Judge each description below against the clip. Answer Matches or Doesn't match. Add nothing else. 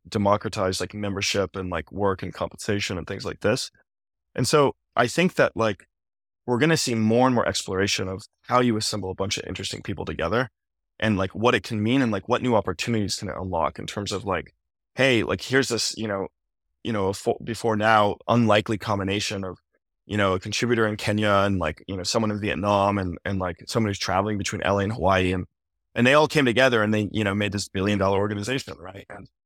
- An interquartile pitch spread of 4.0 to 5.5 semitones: Doesn't match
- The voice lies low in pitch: Matches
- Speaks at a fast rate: Matches